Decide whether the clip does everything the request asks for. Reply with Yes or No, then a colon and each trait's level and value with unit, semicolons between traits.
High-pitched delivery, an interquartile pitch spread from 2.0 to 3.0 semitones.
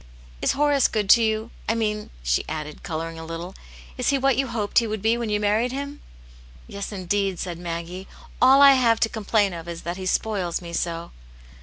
No: high, 205 Hz; average, 5.2 semitones